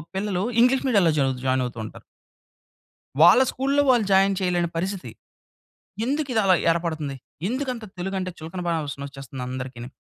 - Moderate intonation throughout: No, wide, 7.8 semitones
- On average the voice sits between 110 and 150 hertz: No, medium, 180 Hz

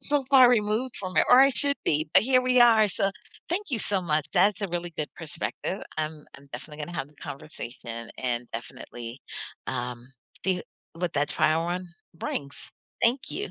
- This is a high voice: No, medium, 175 Hz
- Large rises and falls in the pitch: Yes, wide, 7.9 semitones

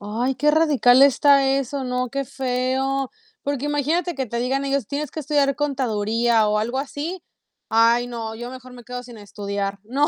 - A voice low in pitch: No, very high, 255 Hz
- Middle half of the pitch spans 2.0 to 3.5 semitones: Yes, average, 3.0 semitones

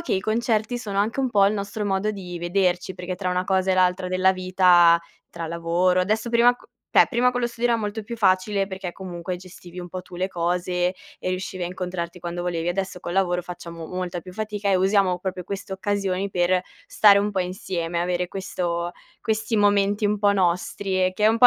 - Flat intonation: Yes, narrow, 2.3 semitones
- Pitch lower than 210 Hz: Yes, medium, 185 Hz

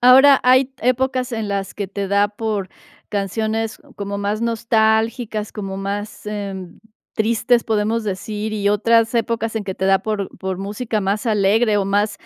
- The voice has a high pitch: Yes, high, 215 Hz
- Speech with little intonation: Yes, narrow, 2.2 semitones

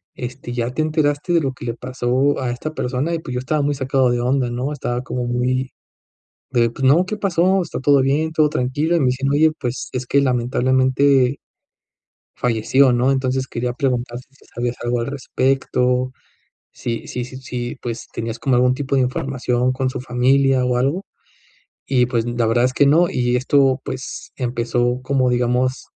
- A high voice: No, low, 130 Hz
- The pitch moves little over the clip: Yes, narrow, 2.1 semitones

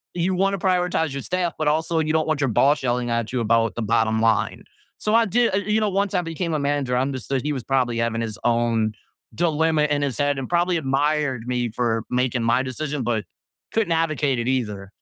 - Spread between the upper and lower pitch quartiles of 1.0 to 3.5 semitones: No, wide, 5.5 semitones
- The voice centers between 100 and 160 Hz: Yes, medium, 140 Hz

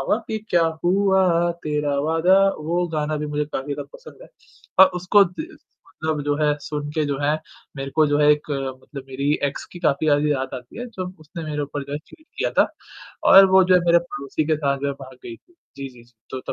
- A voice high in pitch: No, medium, 150 Hz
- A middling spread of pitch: Yes, average, 3.7 semitones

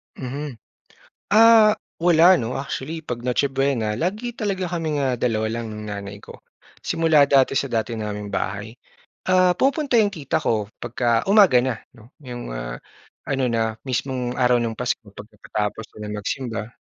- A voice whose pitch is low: Yes, low, 125 Hz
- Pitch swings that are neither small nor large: No, wide, 6.3 semitones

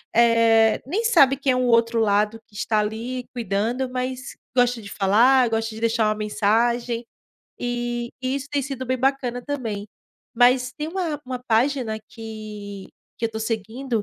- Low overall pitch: No, high, 235 Hz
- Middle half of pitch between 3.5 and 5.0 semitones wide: No, narrow, 2.6 semitones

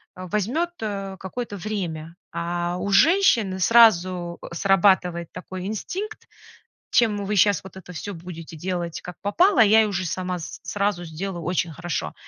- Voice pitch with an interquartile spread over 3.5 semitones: No, average, 3.2 semitones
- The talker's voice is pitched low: No, high, 190 Hz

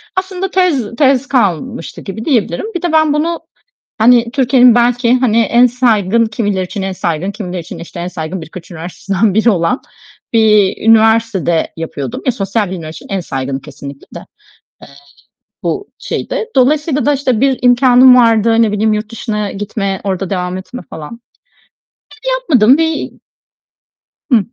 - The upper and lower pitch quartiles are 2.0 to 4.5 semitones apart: No, average, 5.1 semitones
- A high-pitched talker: Yes, high, 220 Hz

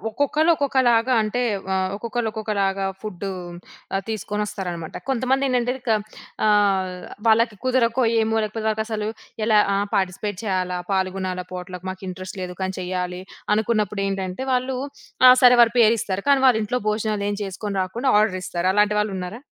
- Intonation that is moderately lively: Yes, average, 3.6 semitones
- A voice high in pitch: Yes, high, 210 Hz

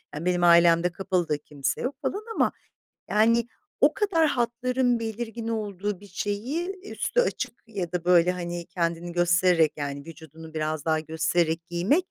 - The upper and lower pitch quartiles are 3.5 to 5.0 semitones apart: No, wide, 5.6 semitones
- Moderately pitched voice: Yes, medium, 180 Hz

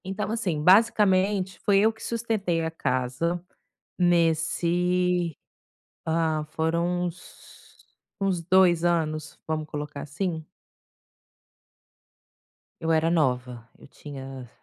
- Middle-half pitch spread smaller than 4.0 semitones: Yes, average, 3.1 semitones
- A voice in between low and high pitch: Yes, medium, 170 Hz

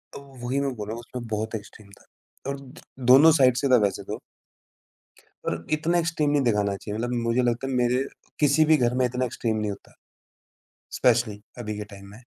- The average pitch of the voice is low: Yes, low, 120 Hz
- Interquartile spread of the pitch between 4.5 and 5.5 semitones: No, average, 3.7 semitones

